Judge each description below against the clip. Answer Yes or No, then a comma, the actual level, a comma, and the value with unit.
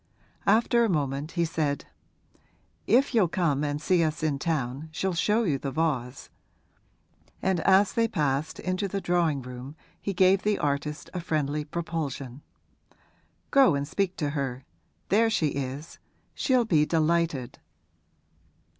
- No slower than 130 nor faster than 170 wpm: Yes, average, 140 wpm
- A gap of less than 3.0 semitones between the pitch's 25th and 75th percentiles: No, average, 4.9 semitones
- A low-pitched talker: No, medium, 160 Hz